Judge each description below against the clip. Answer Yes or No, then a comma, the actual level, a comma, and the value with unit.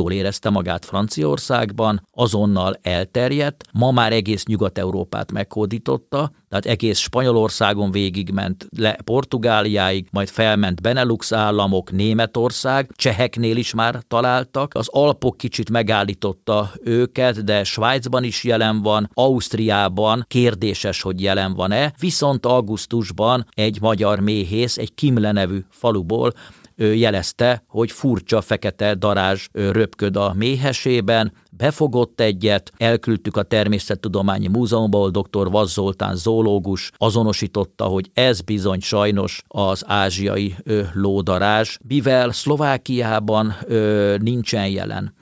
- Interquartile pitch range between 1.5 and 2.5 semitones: No, average, 2.9 semitones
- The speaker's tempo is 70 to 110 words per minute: Yes, slow, 105 wpm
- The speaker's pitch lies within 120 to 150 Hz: No, low, 110 Hz